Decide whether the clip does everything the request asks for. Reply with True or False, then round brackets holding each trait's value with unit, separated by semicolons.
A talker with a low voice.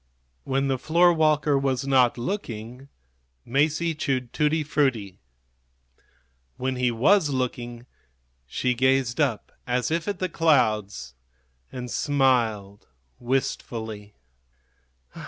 True (130 Hz)